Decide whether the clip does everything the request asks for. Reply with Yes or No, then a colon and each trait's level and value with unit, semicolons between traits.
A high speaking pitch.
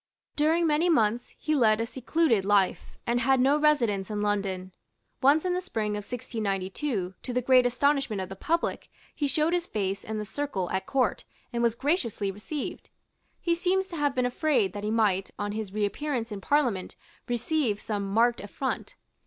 Yes: high, 235 Hz